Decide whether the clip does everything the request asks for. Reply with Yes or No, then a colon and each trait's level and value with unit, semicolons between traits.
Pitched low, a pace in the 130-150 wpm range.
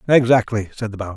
No: low, 110 Hz; fast, 205 wpm